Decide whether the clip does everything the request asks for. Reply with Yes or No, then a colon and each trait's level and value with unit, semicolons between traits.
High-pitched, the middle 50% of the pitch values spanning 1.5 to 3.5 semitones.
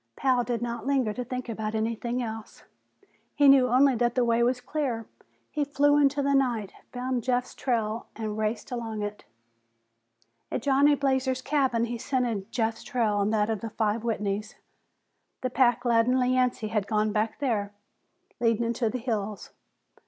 Yes: high, 235 Hz; average, 2.8 semitones